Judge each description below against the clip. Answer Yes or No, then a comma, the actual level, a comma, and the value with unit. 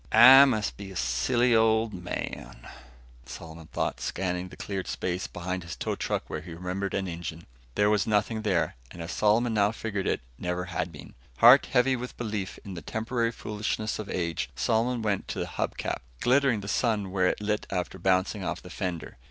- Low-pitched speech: Yes, low, 100 Hz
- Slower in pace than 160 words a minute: No, average, 195 wpm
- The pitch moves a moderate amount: Yes, average, 3.8 semitones